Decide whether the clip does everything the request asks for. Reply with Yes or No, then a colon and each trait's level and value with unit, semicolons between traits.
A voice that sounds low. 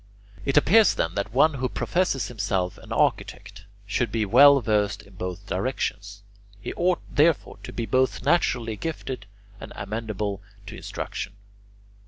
Yes: low, 115 Hz